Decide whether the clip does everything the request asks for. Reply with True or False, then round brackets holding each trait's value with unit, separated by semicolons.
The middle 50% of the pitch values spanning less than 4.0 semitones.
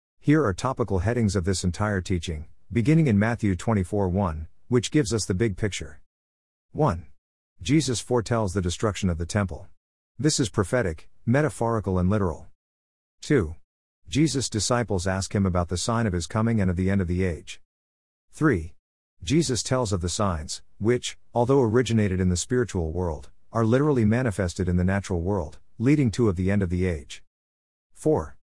False (5.1 semitones)